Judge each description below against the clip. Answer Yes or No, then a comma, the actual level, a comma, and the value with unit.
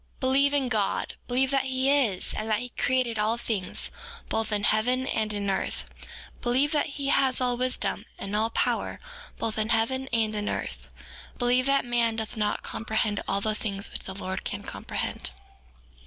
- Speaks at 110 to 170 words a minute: No, average, 185 wpm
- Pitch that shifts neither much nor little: Yes, average, 3.3 semitones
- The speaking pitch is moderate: No, high, 230 Hz